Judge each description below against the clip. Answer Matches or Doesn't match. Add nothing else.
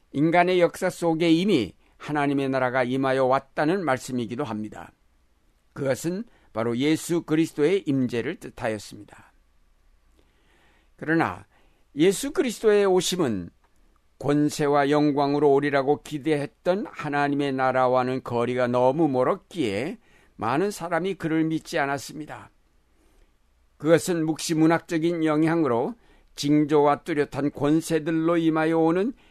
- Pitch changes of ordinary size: Matches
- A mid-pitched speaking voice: Matches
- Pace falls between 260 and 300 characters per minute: Matches